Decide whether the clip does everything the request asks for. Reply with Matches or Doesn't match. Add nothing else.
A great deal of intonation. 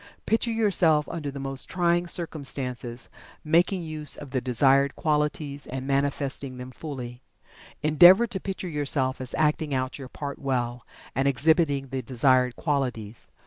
Doesn't match